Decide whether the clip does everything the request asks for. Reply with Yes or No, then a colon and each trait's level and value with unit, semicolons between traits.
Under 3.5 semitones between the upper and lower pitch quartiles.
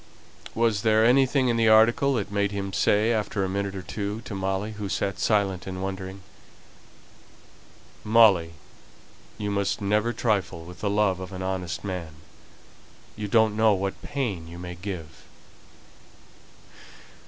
Yes: narrow, 2.6 semitones